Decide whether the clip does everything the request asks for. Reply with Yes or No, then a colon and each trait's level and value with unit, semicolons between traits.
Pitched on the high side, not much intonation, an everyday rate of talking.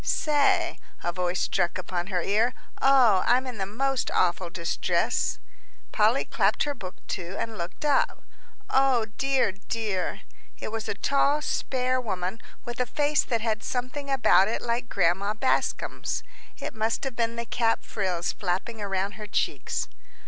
No: high, 225 Hz; average, 5.2 semitones; average, 155 wpm